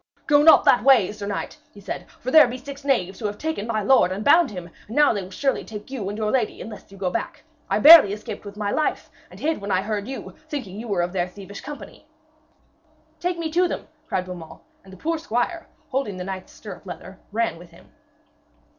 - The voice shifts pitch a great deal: Yes, wide, 6.1 semitones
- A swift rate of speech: Yes, fast, 230 wpm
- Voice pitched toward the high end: Yes, high, 210 Hz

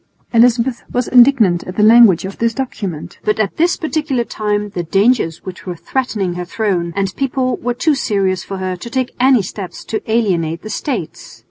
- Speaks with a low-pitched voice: No, high, 215 Hz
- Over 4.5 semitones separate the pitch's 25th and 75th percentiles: Yes, average, 4.9 semitones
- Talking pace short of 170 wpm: No, average, 190 wpm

